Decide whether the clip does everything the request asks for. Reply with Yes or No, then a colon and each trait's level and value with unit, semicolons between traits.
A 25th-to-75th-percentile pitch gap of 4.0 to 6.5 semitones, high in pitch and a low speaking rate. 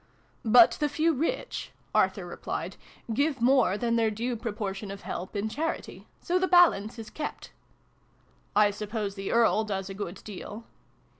No: average, 4.4 semitones; high, 225 Hz; average, 170 wpm